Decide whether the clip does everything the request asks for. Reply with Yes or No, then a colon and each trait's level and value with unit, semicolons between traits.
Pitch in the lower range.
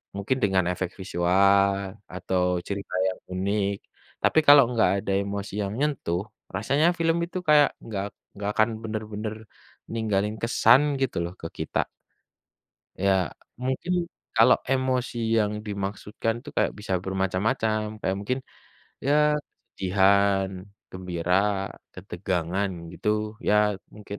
Yes: low, 100 Hz